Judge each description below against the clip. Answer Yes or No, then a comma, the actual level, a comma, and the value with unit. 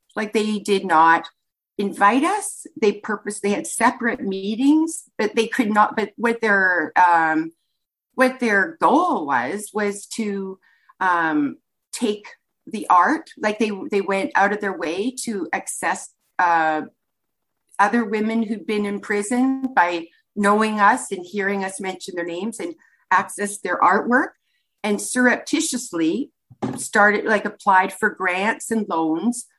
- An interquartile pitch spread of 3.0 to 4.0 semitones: Yes, average, 3.6 semitones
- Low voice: No, high, 210 Hz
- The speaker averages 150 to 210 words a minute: No, average, 140 wpm